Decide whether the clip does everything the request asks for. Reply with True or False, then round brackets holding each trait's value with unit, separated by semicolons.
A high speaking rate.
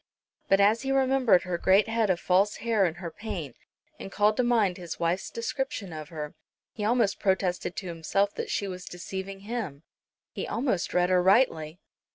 False (185 wpm)